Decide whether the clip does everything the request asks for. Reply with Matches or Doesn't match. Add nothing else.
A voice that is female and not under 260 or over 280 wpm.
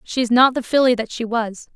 Matches